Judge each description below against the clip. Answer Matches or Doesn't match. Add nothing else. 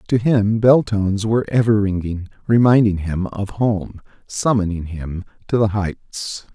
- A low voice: Matches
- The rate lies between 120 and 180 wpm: Matches